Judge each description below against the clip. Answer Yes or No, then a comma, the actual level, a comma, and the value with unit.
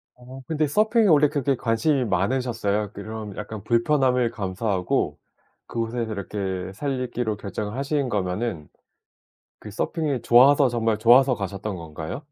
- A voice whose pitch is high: No, low, 115 Hz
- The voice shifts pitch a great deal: No, average, 4.6 semitones